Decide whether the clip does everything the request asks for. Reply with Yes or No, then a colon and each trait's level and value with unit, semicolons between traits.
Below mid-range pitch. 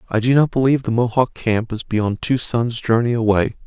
Yes: low, 120 Hz